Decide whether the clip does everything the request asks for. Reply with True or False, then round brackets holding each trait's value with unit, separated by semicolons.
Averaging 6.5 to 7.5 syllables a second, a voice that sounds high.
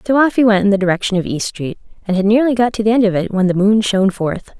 True (6.7 syllables/s; 205 Hz)